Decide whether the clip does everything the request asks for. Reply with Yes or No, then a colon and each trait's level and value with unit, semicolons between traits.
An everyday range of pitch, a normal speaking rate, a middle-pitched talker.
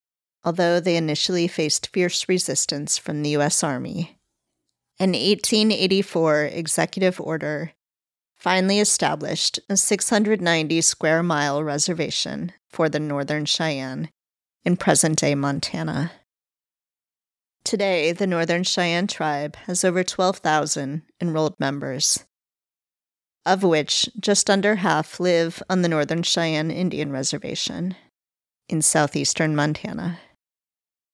No: average, 3.6 semitones; slow, 105 wpm; medium, 165 Hz